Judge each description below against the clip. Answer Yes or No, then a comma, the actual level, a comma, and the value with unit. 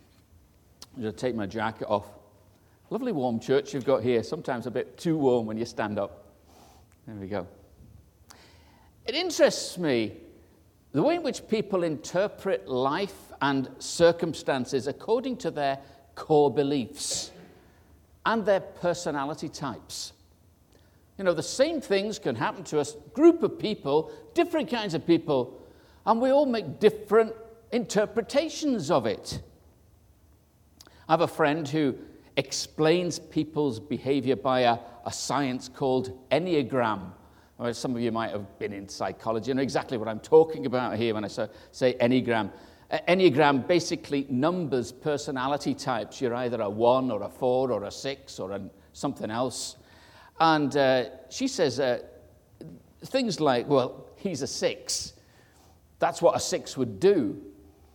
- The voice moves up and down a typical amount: No, wide, 8.2 semitones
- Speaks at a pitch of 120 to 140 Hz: Yes, low, 135 Hz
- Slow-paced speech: No, average, 145 wpm